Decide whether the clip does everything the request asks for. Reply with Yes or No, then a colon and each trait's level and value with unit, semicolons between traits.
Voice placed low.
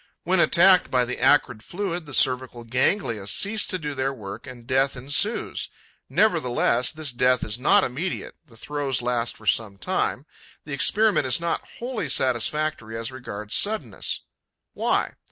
Yes: low, 130 Hz